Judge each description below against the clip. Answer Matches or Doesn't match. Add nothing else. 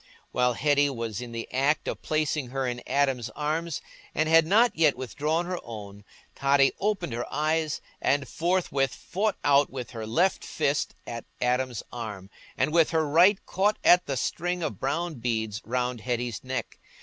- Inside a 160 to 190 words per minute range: Matches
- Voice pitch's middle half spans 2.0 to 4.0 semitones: Doesn't match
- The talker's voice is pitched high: Doesn't match